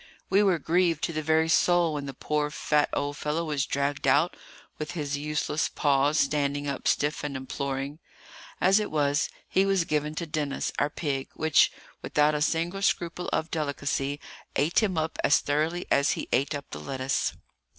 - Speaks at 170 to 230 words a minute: Yes, average, 180 wpm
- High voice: No, medium, 150 Hz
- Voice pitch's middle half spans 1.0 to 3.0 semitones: Yes, narrow, 2.5 semitones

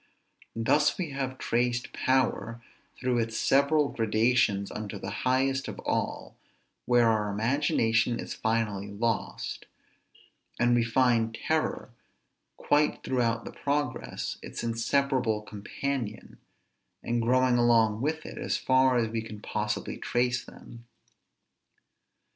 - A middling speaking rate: No, slow, 120 wpm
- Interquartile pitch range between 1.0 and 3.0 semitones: Yes, narrow, 2.6 semitones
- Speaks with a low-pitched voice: Yes, low, 120 Hz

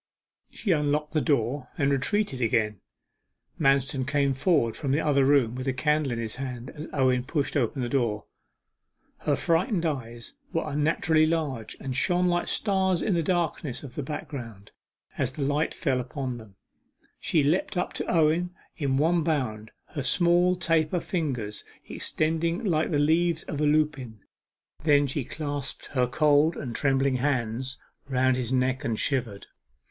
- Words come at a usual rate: Yes, average, 160 wpm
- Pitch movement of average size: Yes, average, 3.8 semitones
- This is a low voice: No, medium, 145 Hz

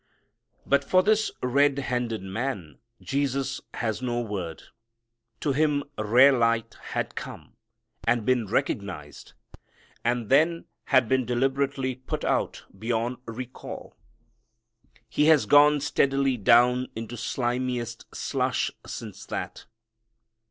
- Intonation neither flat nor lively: Yes, average, 3.1 semitones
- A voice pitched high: No, low, 125 Hz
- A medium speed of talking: No, slow, 110 wpm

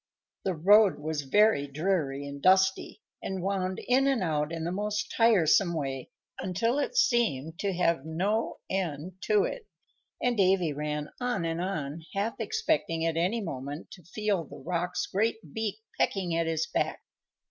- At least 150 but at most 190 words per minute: Yes, average, 160 wpm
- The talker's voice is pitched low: No, medium, 185 Hz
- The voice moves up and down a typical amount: Yes, average, 4.8 semitones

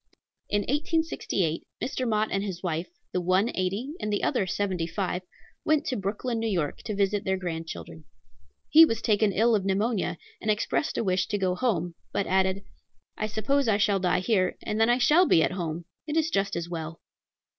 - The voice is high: Yes, high, 200 Hz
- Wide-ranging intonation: No, average, 3.9 semitones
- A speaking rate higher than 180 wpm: Yes, average, 190 wpm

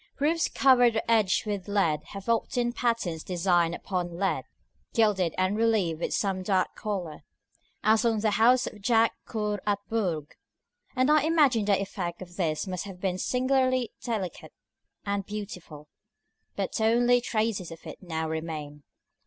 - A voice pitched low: No, high, 205 Hz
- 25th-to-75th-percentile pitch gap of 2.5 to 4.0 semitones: No, average, 4.4 semitones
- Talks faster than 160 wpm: No, average, 155 wpm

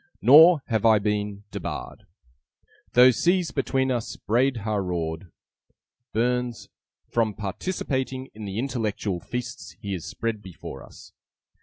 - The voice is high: No, low, 115 Hz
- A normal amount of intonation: Yes, average, 4.1 semitones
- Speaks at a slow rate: Yes, slow, 125 wpm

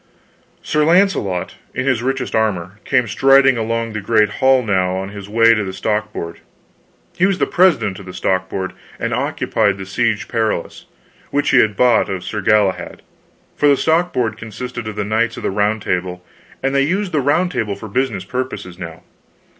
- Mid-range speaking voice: No, low, 110 Hz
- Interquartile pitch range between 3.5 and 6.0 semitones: Yes, average, 5.1 semitones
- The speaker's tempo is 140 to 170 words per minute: No, average, 185 wpm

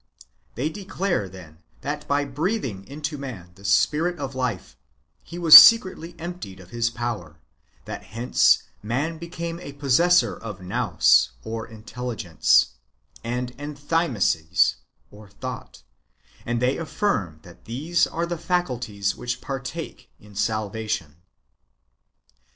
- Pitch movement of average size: No, wide, 7.6 semitones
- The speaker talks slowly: Yes, slow, 115 wpm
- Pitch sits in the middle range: No, low, 125 Hz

